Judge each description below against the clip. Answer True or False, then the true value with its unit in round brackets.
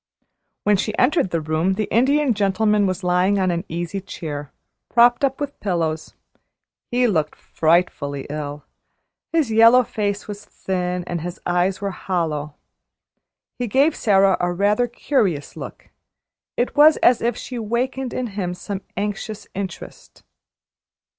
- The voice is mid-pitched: False (195 Hz)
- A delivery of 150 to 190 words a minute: False (140 wpm)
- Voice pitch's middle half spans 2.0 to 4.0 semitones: False (5.0 semitones)